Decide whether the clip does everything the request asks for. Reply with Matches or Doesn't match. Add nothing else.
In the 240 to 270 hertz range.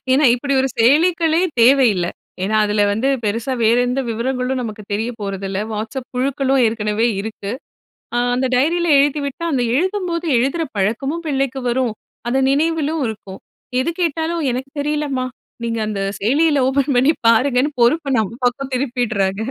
Matches